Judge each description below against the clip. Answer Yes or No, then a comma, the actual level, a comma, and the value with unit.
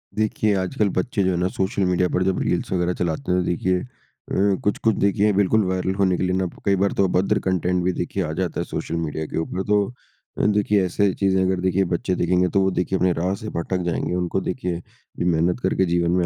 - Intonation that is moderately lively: No, narrow, 1.6 semitones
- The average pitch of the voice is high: No, very low, 95 Hz